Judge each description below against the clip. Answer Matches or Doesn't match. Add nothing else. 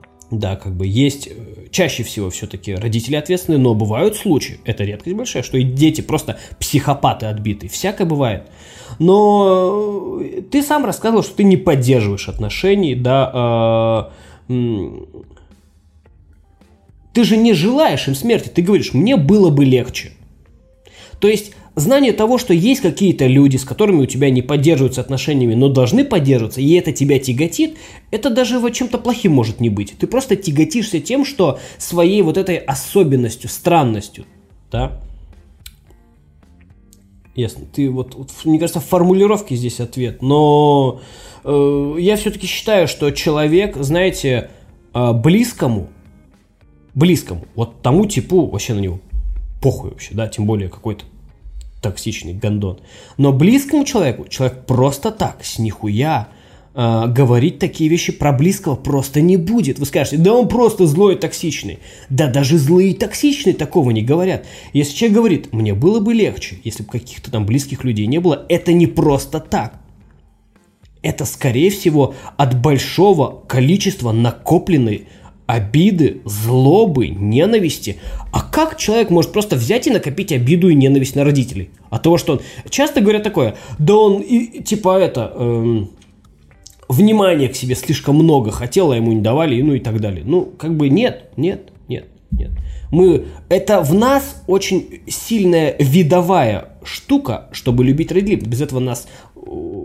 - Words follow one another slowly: Doesn't match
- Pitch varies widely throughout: Matches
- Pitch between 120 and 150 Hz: Matches